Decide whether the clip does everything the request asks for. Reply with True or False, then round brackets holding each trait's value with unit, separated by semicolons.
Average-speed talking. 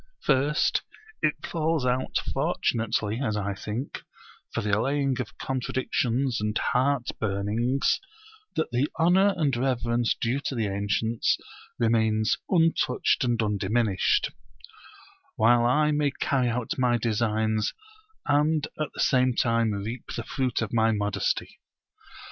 False (125 wpm)